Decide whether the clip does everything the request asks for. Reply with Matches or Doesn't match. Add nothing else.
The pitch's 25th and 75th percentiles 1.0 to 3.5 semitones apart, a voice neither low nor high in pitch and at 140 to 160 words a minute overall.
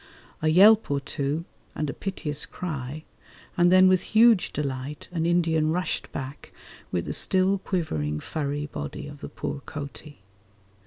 Doesn't match